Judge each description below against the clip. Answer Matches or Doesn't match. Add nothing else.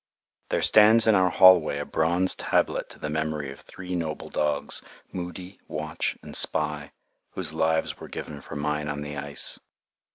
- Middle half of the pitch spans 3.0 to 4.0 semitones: Matches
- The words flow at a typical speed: Matches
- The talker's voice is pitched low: Matches